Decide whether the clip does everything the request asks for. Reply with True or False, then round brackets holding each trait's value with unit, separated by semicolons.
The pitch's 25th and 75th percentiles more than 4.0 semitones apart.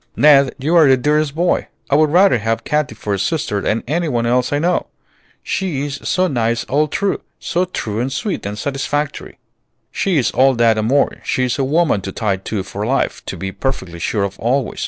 True (5.3 semitones)